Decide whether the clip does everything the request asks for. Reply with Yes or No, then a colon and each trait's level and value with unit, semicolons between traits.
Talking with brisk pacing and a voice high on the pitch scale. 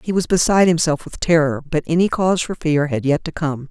No: fast, 245 wpm; medium, 160 Hz